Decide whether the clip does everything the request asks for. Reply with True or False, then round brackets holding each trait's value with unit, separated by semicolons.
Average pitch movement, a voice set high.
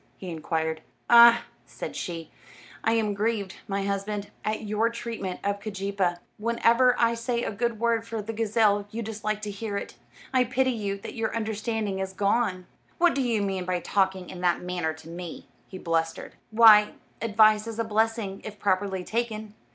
True (3.0 semitones; 210 Hz)